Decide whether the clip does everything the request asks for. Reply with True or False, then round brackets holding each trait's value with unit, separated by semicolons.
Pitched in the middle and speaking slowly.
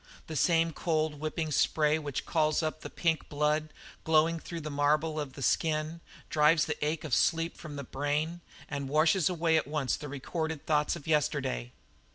False (155 Hz; 185 wpm)